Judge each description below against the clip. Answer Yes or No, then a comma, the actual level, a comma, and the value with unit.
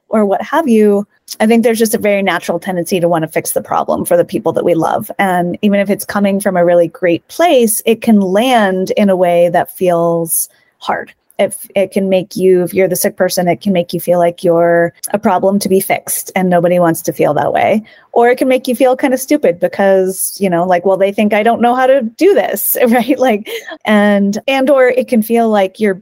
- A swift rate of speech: Yes, fast, 240 wpm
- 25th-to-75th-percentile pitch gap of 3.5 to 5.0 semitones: Yes, average, 4.5 semitones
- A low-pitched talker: No, high, 200 Hz